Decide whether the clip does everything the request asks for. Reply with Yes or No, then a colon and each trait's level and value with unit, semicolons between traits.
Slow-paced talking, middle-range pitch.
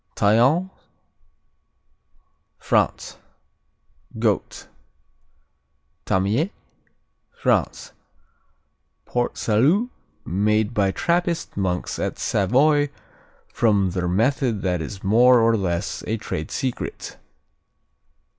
No: slow, 80 wpm; low, 110 Hz